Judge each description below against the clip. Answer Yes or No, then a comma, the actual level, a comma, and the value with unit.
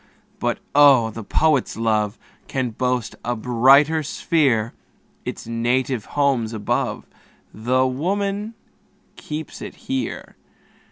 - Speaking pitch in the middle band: No, low, 130 Hz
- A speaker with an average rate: No, slow, 105 wpm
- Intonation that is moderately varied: Yes, average, 4.6 semitones